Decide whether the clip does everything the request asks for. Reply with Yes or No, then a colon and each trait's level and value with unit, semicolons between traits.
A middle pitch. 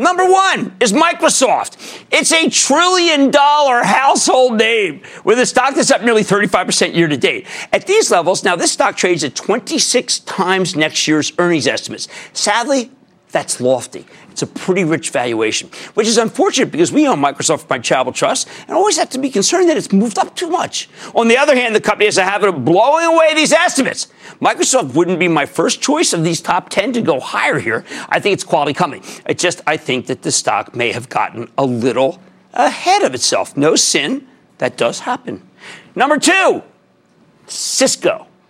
No: high, 245 Hz